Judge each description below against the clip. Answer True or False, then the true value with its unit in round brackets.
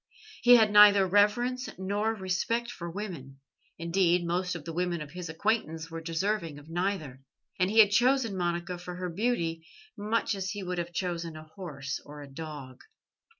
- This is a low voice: False (180 Hz)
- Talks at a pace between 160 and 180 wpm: True (175 wpm)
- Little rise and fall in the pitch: False (3.9 semitones)